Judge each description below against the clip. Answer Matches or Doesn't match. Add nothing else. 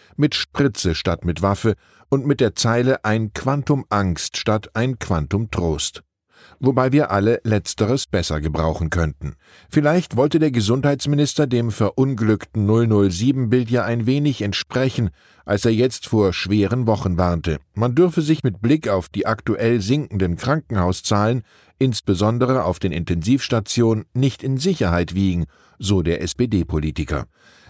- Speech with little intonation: Doesn't match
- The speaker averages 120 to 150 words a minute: Matches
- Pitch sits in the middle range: Doesn't match